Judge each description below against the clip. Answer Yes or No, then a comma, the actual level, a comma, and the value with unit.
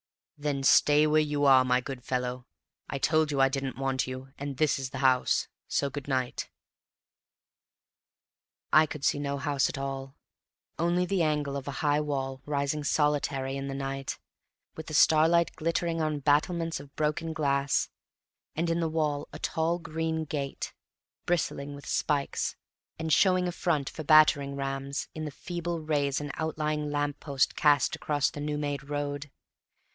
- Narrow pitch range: Yes, narrow, 2.3 semitones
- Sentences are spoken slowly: No, average, 165 wpm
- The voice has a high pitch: No, medium, 145 Hz